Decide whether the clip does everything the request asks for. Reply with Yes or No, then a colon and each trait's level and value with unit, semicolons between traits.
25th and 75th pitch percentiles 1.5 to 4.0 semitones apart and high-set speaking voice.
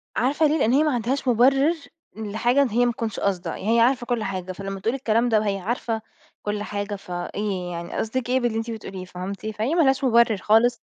Yes: average, 3.6 semitones; high, 225 Hz